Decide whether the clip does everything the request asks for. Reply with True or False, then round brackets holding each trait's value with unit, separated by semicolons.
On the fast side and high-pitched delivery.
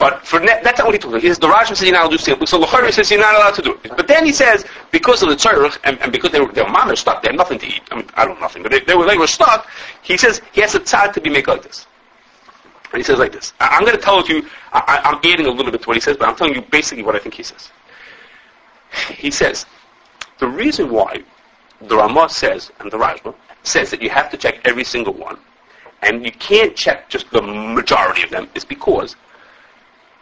True (275 wpm; 310 Hz)